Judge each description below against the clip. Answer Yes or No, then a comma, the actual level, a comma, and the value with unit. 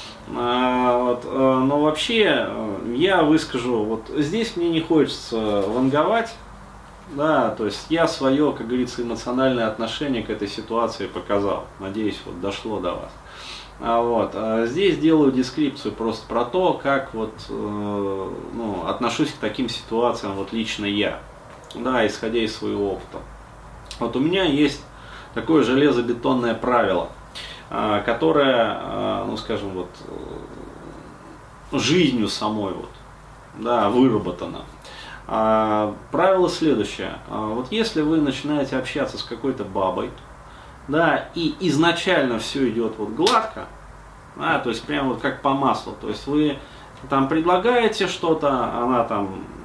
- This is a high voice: No, low, 120 Hz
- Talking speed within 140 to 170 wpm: No, average, 125 wpm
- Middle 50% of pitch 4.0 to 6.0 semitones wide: Yes, average, 5.1 semitones